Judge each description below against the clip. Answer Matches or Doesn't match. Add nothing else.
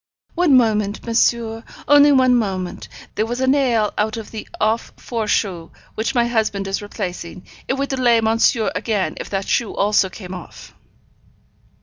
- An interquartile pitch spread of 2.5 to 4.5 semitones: Matches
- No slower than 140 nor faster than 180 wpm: Matches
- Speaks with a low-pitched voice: Doesn't match